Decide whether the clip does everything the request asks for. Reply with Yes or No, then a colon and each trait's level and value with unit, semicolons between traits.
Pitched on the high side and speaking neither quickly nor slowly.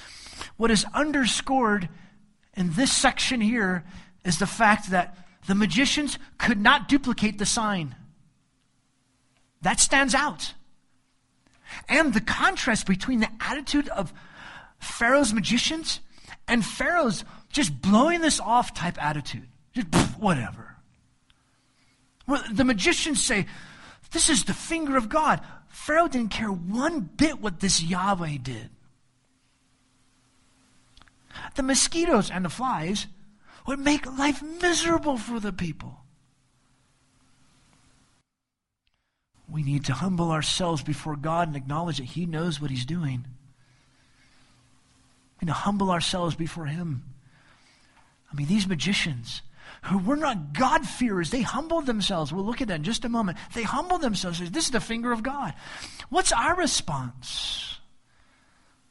No: high, 195 Hz; slow, 130 wpm